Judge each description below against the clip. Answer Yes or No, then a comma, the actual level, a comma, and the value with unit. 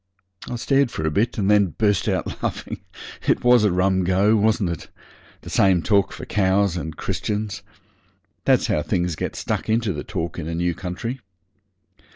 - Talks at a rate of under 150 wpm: No, average, 180 wpm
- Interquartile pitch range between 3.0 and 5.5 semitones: Yes, average, 3.6 semitones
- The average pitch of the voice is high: No, very low, 95 Hz